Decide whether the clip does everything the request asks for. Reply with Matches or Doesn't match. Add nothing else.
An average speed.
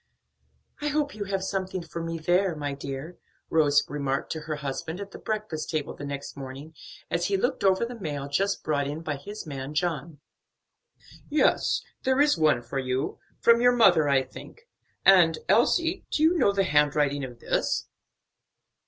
Matches